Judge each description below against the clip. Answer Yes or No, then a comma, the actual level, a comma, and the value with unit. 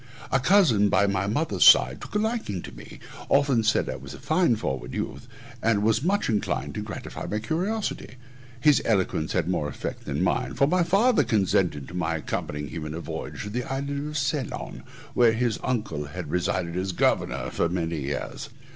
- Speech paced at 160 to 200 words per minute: Yes, average, 185 wpm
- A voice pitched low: Yes, low, 105 Hz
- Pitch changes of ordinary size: No, wide, 8.7 semitones